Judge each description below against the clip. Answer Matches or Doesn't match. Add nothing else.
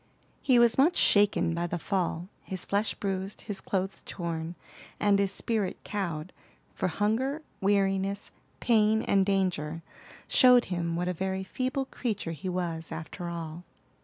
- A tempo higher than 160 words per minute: Doesn't match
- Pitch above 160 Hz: Matches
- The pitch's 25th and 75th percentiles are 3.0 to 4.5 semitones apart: Matches